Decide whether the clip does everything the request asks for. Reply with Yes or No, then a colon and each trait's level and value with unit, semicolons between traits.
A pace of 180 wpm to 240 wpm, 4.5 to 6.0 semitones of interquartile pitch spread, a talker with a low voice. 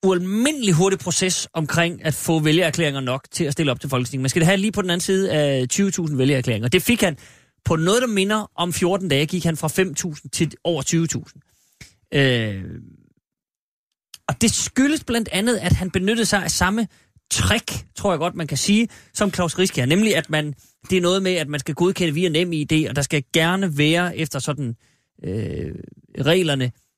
No: average, 200 wpm; average, 5.0 semitones; medium, 165 Hz